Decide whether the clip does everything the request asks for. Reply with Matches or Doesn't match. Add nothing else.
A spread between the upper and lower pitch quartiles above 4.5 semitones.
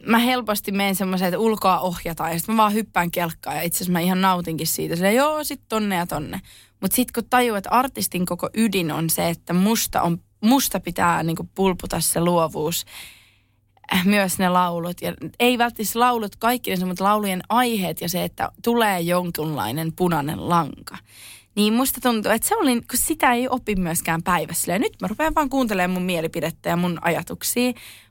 Matches